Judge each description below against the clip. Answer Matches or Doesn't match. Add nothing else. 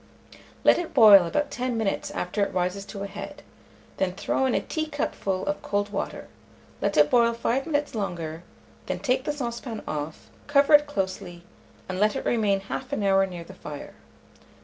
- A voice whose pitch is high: Matches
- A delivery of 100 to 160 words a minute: Doesn't match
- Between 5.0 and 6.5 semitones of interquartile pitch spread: Matches